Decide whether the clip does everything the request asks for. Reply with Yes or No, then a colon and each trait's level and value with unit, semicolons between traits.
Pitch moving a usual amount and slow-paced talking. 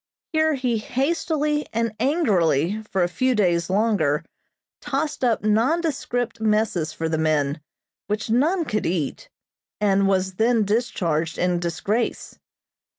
No: wide, 6.3 semitones; slow, 125 wpm